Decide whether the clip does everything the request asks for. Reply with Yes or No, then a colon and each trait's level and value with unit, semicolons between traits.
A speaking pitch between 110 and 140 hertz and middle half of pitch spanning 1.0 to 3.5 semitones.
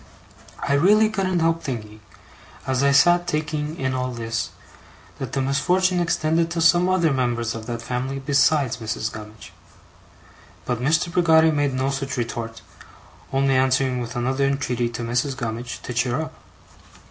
No: low, 135 Hz; average, 4.8 semitones